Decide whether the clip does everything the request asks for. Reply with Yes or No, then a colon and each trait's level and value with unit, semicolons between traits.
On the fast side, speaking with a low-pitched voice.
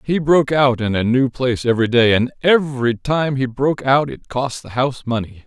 Yes: fast, 220 wpm; low, 130 Hz